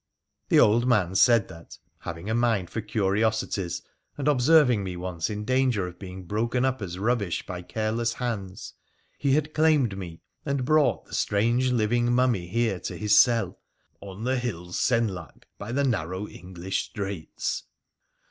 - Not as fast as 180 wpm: Yes, average, 160 wpm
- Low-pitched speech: Yes, low, 110 Hz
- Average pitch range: Yes, average, 4.6 semitones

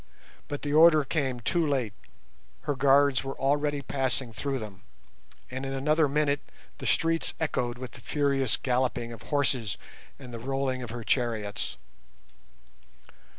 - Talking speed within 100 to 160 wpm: Yes, average, 145 wpm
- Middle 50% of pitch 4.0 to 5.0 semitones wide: No, average, 3.0 semitones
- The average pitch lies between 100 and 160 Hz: Yes, low, 135 Hz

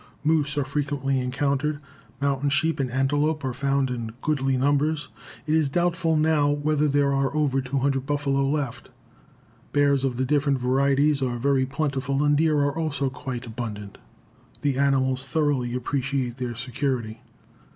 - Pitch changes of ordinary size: No, narrow, 1.9 semitones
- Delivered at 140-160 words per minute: Yes, average, 150 wpm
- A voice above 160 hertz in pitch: No, medium, 140 Hz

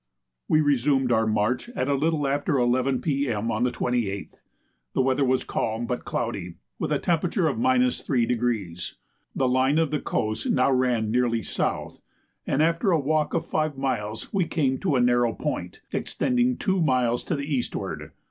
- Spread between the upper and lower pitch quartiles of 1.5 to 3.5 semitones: No, average, 4.3 semitones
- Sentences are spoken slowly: No, average, 165 wpm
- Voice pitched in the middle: No, low, 130 Hz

